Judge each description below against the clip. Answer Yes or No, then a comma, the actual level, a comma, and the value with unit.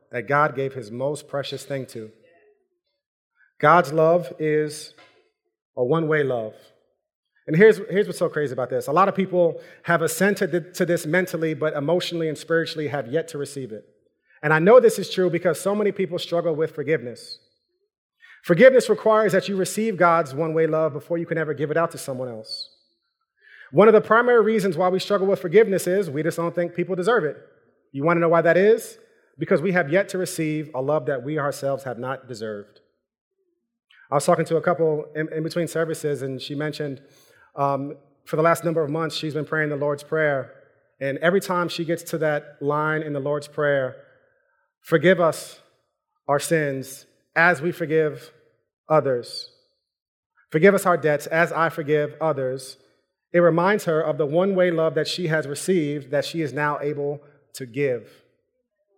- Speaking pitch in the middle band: Yes, medium, 165 Hz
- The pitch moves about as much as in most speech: Yes, average, 4.2 semitones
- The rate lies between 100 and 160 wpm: No, average, 185 wpm